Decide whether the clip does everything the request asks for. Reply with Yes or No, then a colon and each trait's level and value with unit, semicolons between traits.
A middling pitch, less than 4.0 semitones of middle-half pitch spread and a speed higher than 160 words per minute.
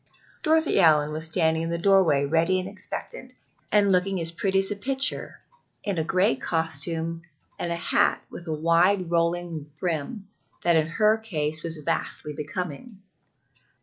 No: medium, 170 Hz; average, 3.2 semitones; average, 155 wpm